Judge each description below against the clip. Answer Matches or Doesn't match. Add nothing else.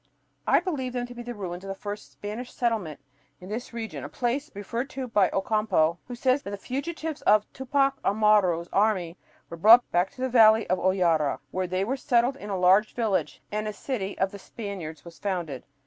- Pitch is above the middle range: Matches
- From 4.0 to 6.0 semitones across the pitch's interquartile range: Matches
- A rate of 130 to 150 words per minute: Doesn't match